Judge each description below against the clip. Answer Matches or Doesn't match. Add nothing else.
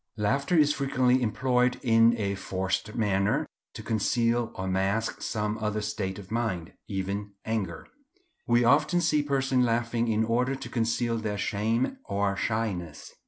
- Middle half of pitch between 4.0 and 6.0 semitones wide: Doesn't match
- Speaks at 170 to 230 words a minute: Doesn't match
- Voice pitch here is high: Doesn't match